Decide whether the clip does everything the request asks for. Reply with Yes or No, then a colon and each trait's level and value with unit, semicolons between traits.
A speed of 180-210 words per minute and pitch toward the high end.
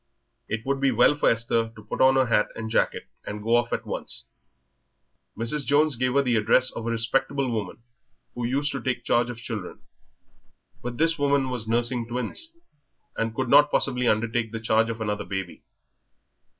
No: average, 185 wpm; low, 120 Hz